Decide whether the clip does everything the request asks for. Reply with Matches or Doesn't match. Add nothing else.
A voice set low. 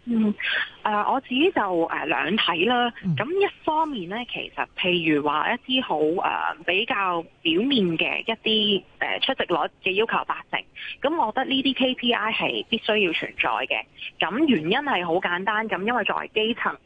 Doesn't match